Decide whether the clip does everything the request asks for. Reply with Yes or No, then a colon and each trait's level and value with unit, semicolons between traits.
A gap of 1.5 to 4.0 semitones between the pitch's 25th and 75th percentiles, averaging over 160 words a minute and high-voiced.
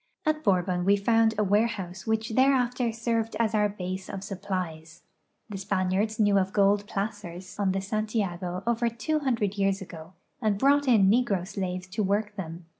Yes: average, 3.1 semitones; average, 170 wpm; high, 205 Hz